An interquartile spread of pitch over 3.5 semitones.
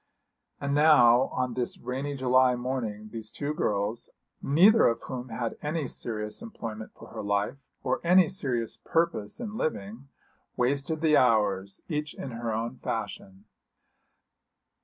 Yes: average, 4.9 semitones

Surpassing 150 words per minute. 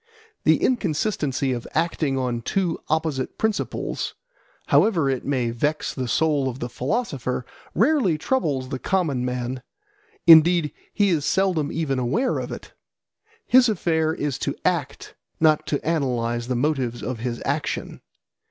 No: average, 140 wpm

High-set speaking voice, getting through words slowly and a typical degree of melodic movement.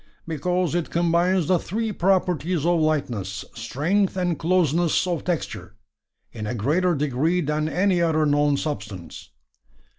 No: medium, 160 Hz; slow, 130 wpm; average, 4.0 semitones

